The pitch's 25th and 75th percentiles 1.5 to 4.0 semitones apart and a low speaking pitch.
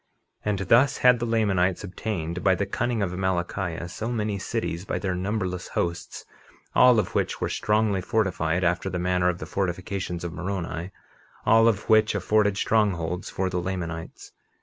Yes: average, 3.2 semitones; very low, 95 Hz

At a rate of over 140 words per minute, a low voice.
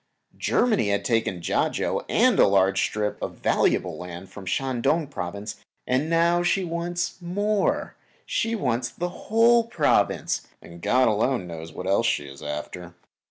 Yes: average, 160 wpm; low, 120 Hz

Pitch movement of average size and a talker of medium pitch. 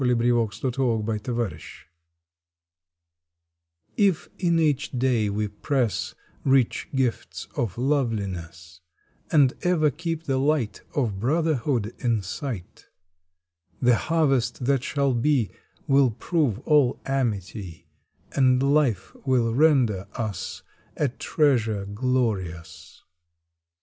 No: average, 4.6 semitones; low, 125 Hz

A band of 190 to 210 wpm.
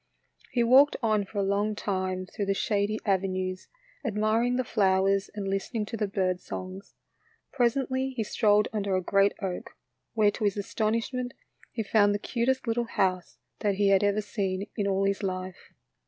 No: average, 175 wpm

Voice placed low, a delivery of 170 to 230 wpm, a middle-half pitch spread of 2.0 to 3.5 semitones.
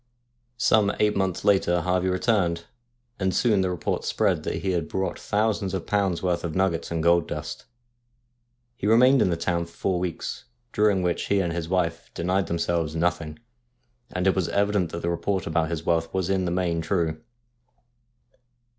Yes: very low, 90 Hz; average, 180 wpm; narrow, 2.4 semitones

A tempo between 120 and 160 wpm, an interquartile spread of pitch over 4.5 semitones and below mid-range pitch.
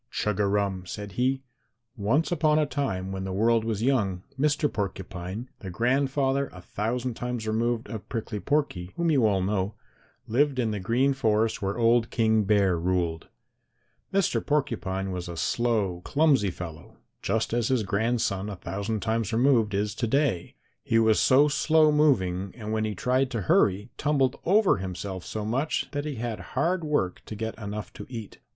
No: average, 175 wpm; average, 5.2 semitones; low, 110 Hz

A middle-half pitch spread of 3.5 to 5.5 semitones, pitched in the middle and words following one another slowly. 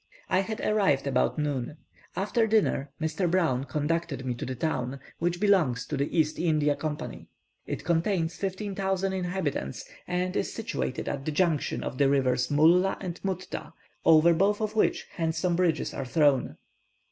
No: average, 4.7 semitones; medium, 165 Hz; average, 160 wpm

